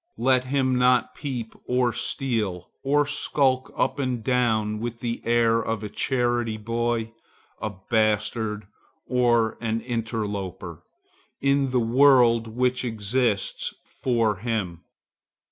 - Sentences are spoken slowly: Yes, slow, 115 wpm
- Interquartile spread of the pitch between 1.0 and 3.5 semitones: Yes, narrow, 2.4 semitones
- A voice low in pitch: Yes, low, 120 Hz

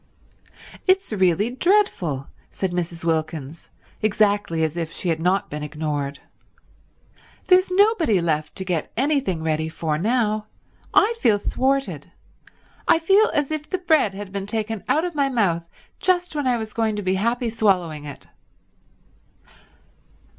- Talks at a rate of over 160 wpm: No, average, 145 wpm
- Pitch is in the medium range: No, high, 205 Hz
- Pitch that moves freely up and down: Yes, wide, 8.7 semitones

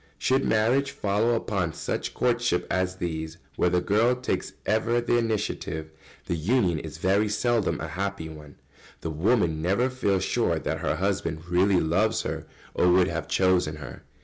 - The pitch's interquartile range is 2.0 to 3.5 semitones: No, average, 5.2 semitones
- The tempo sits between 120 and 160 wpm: No, average, 170 wpm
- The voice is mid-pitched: No, very low, 95 Hz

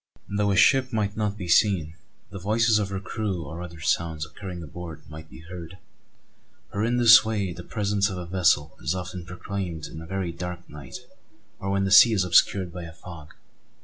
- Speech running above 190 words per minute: Yes, average, 200 wpm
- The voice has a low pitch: Yes, very low, 90 Hz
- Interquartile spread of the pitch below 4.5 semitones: Yes, average, 3.3 semitones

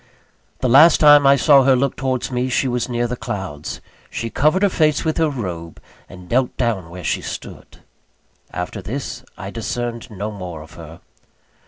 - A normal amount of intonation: No, wide, 6.5 semitones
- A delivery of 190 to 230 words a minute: No, average, 180 wpm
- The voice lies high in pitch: No, low, 120 Hz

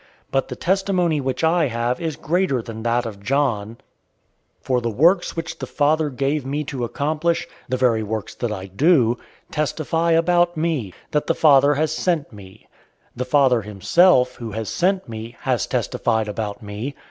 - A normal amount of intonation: No, wide, 5.7 semitones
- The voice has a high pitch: No, low, 135 Hz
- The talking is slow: No, average, 170 wpm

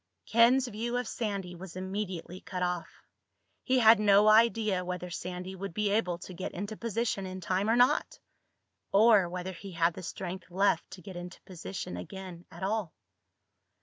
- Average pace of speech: Yes, average, 165 wpm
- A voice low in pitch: No, high, 190 Hz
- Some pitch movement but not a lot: Yes, average, 3.1 semitones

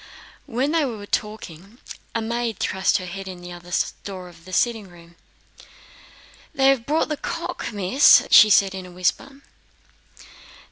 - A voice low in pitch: No, high, 205 Hz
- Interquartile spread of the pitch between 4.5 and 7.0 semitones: Yes, average, 4.8 semitones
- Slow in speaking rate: No, average, 160 wpm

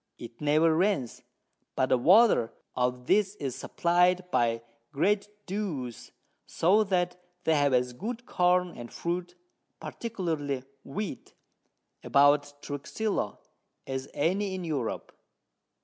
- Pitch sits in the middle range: Yes, medium, 160 Hz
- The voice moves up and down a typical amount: No, wide, 6.0 semitones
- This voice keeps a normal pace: No, slow, 115 wpm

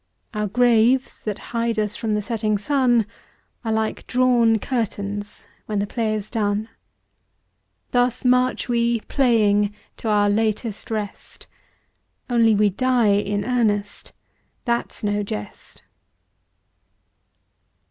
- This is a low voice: No, high, 220 Hz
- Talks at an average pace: No, slow, 115 wpm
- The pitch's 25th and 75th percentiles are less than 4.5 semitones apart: Yes, narrow, 2.5 semitones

